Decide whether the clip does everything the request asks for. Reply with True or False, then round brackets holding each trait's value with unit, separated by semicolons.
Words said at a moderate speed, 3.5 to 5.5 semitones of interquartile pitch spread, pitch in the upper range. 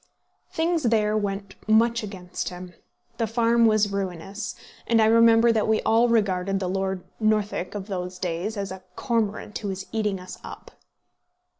False (160 wpm; 2.9 semitones; 210 Hz)